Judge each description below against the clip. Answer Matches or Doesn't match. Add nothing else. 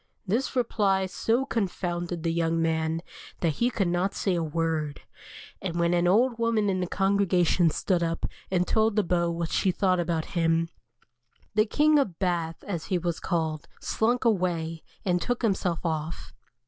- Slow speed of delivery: Doesn't match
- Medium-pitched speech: Matches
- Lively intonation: Doesn't match